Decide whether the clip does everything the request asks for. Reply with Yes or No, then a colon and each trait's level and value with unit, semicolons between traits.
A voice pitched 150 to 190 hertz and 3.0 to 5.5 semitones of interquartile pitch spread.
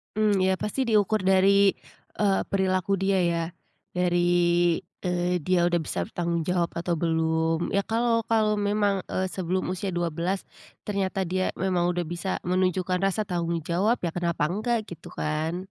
No: medium, 185 Hz; narrow, 2.4 semitones